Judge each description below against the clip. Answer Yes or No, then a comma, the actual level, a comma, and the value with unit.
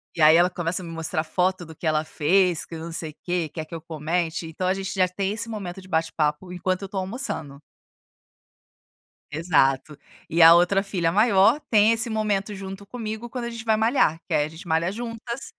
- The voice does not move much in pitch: No, average, 4.1 semitones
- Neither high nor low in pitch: Yes, medium, 180 Hz